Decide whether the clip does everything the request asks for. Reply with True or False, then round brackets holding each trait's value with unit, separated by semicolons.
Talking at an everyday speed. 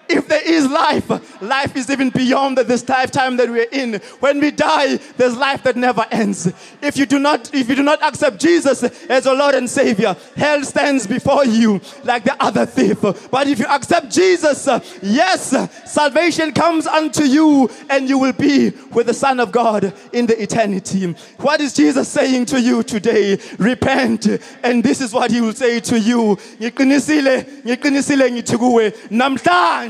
True (170 wpm)